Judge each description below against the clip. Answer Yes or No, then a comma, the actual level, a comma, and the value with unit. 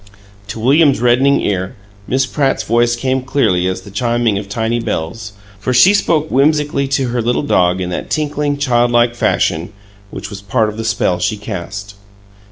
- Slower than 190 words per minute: Yes, average, 175 wpm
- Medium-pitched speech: No, low, 120 Hz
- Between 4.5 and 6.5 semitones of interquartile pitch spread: Yes, average, 4.9 semitones